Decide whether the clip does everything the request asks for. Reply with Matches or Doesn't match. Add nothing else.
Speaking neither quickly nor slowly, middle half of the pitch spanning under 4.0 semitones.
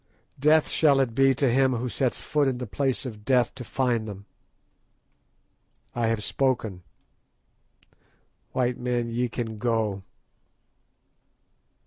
Doesn't match